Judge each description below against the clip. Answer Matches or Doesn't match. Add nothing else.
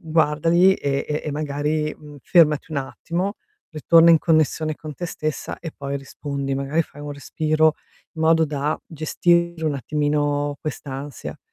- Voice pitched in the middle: Matches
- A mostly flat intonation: Matches